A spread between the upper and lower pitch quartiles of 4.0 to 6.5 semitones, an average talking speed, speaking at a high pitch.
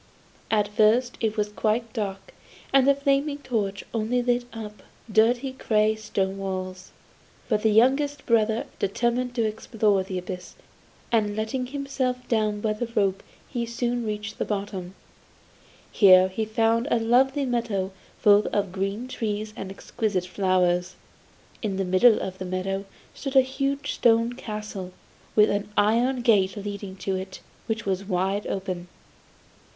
No: average, 3.6 semitones; average, 145 wpm; high, 215 Hz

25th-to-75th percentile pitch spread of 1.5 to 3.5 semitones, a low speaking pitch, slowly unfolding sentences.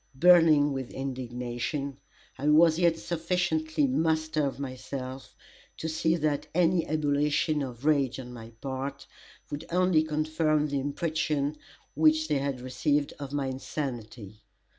No: average, 2.9 semitones; medium, 145 Hz; slow, 130 wpm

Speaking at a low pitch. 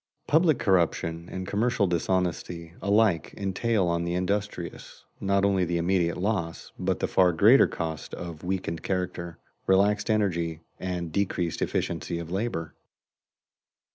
Yes: very low, 90 Hz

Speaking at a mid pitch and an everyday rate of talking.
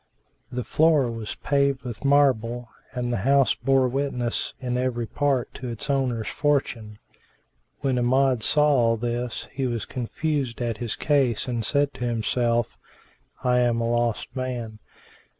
No: low, 125 Hz; average, 150 wpm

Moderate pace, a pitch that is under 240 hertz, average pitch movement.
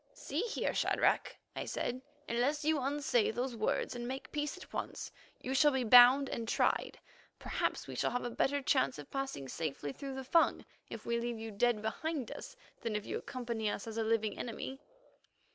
No: average, 195 wpm; high, 245 Hz; average, 3.5 semitones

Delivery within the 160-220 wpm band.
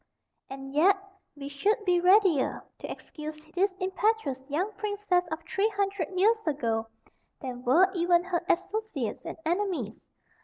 No: average, 140 wpm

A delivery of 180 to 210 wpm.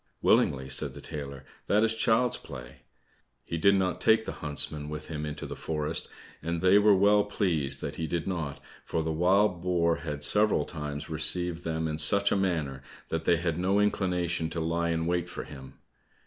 Yes: average, 190 wpm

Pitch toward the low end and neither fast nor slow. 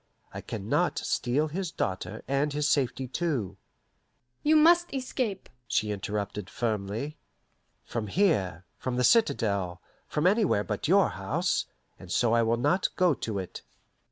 Yes: low, 125 Hz; average, 150 wpm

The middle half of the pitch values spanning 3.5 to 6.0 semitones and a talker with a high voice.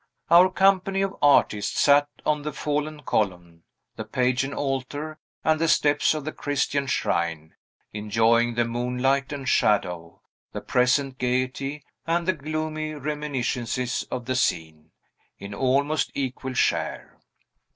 No: average, 4.0 semitones; low, 135 Hz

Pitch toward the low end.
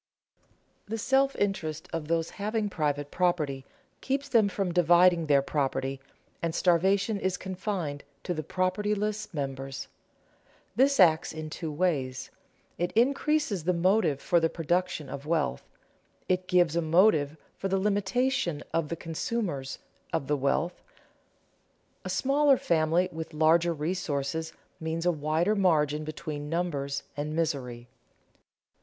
No: medium, 170 Hz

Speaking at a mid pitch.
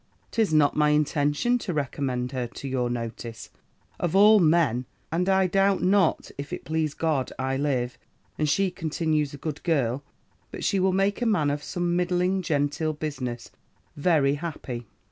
Yes: medium, 155 Hz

